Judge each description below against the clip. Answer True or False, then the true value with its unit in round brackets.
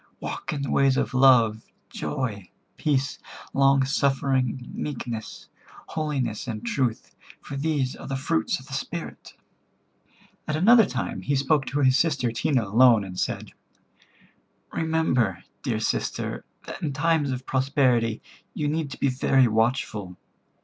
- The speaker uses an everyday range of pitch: True (3.3 semitones)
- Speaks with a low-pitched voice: True (130 Hz)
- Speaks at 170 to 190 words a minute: False (140 wpm)